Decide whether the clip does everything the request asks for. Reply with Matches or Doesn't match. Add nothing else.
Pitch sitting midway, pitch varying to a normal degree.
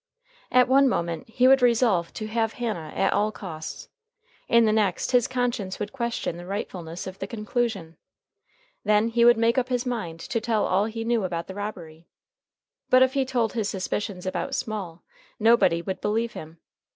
Doesn't match